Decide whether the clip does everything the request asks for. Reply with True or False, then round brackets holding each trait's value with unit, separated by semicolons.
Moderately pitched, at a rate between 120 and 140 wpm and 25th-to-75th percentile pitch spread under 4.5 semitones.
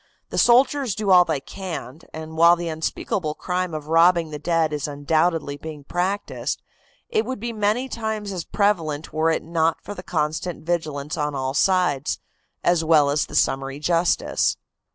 False (165 Hz; 170 wpm; 3.4 semitones)